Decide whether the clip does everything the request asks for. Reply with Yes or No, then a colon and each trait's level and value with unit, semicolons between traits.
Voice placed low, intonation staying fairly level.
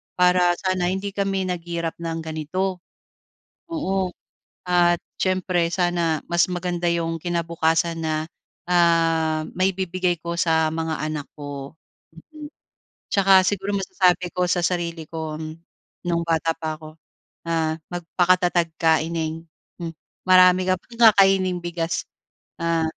No: medium, 175 Hz; narrow, 2.0 semitones